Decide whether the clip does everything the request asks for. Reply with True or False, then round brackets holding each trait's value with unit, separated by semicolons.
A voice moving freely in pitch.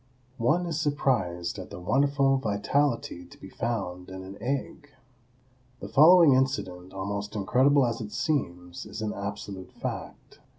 True (6.4 semitones)